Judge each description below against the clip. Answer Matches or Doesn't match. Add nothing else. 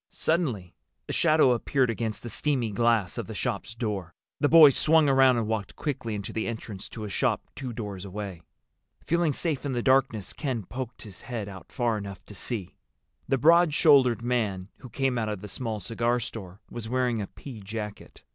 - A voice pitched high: Doesn't match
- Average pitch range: Matches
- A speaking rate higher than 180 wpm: Matches